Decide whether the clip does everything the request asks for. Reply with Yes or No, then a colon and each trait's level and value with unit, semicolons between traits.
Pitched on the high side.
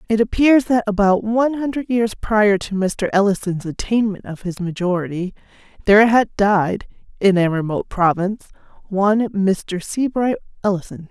Yes: high, 205 Hz